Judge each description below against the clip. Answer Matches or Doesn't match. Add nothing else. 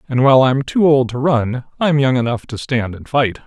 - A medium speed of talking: Doesn't match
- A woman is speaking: Doesn't match